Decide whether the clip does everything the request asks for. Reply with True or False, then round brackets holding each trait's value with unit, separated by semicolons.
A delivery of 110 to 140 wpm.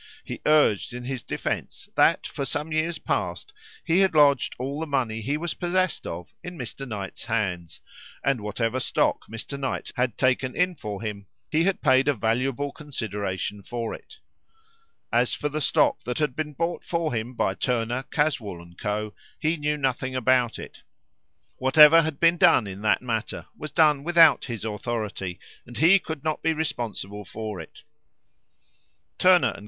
False (170 wpm)